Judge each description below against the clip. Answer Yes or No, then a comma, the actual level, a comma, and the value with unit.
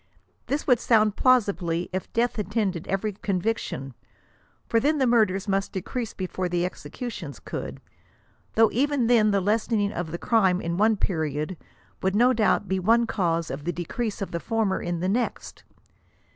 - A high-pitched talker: Yes, high, 200 Hz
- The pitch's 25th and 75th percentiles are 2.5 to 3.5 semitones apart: No, average, 4.3 semitones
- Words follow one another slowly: No, average, 165 wpm